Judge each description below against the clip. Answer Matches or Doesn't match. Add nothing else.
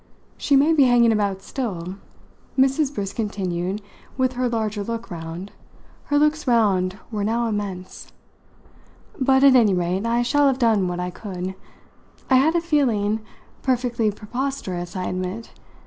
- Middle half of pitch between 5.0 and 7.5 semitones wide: Matches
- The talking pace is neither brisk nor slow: Matches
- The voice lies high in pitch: Matches